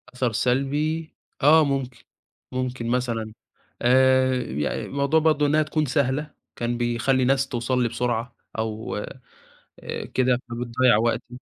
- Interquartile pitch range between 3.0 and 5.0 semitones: No, narrow, 2.6 semitones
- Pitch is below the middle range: Yes, low, 130 Hz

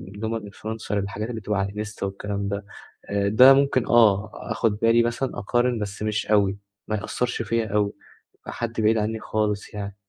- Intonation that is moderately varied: No, narrow, 2.1 semitones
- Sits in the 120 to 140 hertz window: No, low, 105 Hz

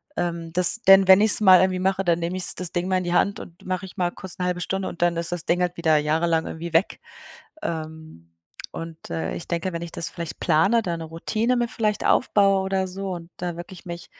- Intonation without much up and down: Yes, narrow, 2.3 semitones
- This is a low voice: No, medium, 175 Hz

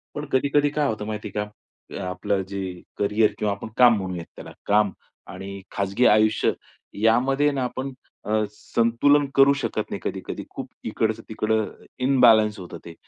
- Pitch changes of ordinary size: Yes, average, 4.0 semitones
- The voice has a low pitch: Yes, low, 110 Hz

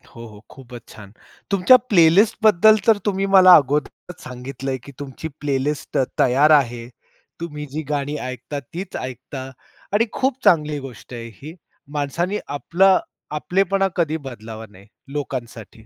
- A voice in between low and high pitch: Yes, medium, 145 Hz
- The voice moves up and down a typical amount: No, wide, 5.8 semitones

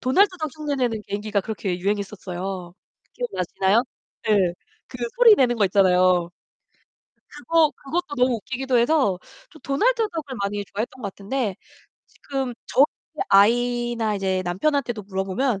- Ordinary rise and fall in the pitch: No, wide, 5.8 semitones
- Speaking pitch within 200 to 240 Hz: Yes, high, 230 Hz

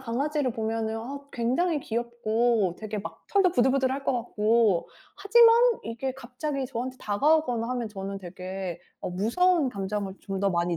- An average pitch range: Yes, average, 4.7 semitones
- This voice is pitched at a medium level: No, high, 235 Hz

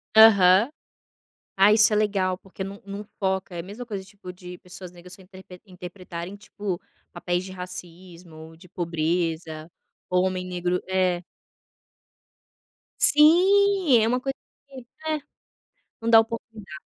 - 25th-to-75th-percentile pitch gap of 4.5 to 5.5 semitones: No, average, 3.1 semitones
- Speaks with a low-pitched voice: No, medium, 185 Hz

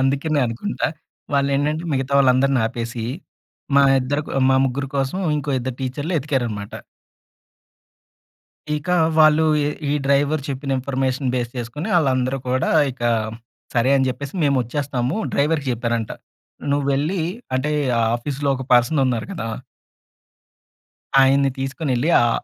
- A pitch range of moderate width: No, narrow, 2.3 semitones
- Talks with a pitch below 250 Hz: Yes, low, 135 Hz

